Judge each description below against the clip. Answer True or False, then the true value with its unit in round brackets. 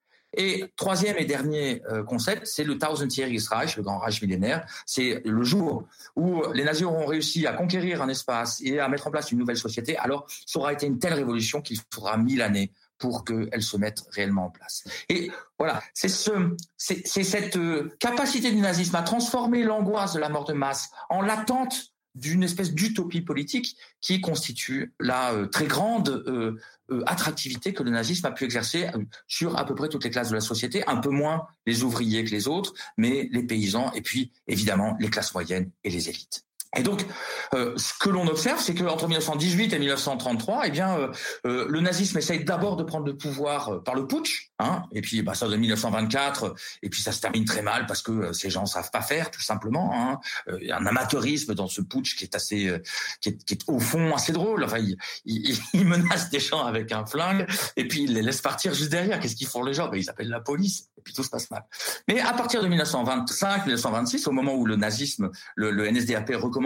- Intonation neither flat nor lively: False (7.4 semitones)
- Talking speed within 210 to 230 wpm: True (220 wpm)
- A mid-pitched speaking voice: True (145 Hz)